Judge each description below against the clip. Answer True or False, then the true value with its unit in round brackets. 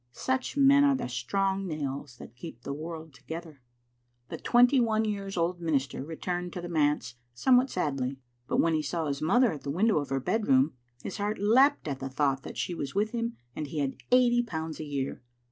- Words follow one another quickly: True (210 wpm)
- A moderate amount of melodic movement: False (7.5 semitones)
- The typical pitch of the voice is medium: True (165 Hz)